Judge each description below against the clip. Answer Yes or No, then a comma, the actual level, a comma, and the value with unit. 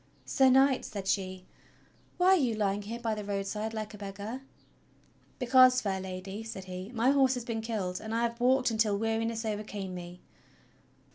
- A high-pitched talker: Yes, high, 220 Hz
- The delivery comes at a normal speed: Yes, average, 185 wpm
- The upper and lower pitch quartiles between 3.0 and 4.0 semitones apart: Yes, average, 3.4 semitones